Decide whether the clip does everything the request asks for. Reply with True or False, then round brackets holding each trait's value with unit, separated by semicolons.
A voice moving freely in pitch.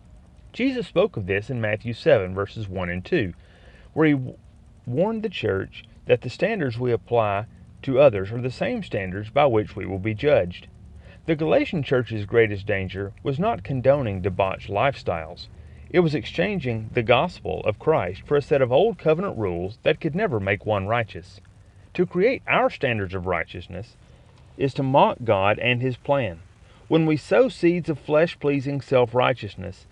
True (7.1 semitones)